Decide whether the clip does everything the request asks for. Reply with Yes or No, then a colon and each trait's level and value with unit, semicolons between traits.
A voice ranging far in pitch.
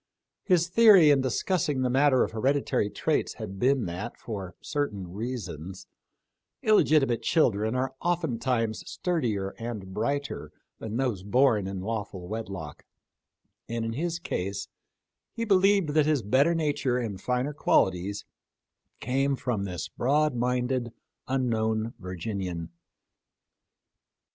Yes: wide, 5.8 semitones